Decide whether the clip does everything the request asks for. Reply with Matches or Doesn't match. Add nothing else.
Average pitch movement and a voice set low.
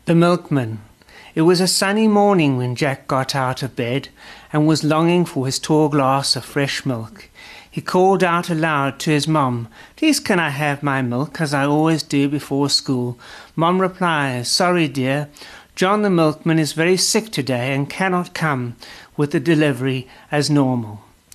Doesn't match